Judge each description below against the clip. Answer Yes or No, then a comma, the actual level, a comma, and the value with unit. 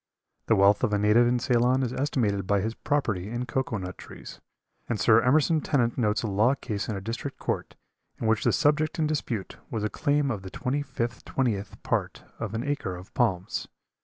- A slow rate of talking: No, fast, 205 wpm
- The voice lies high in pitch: No, low, 115 Hz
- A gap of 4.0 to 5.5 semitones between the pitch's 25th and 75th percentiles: Yes, average, 4.4 semitones